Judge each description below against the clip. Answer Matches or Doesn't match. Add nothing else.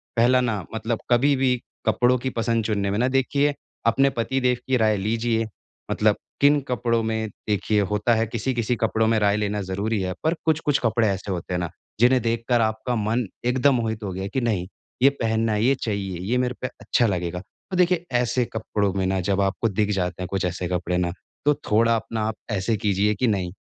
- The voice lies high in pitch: Doesn't match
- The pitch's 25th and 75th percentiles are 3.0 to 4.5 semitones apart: Matches